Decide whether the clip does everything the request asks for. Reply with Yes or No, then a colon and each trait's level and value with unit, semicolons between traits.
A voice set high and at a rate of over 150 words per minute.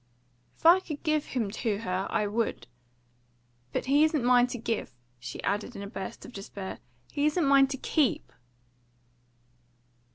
Yes: high, 245 Hz; average, 160 wpm